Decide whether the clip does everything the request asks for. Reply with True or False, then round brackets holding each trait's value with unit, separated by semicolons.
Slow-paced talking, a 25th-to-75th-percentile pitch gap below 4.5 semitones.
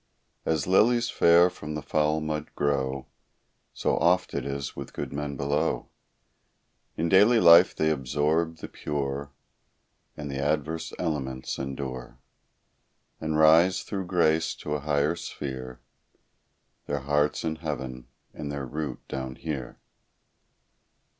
True (125 wpm; 2.9 semitones)